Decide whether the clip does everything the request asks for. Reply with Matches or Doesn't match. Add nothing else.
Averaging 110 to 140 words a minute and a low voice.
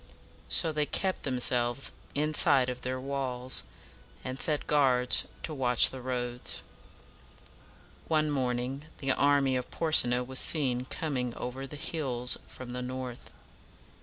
Matches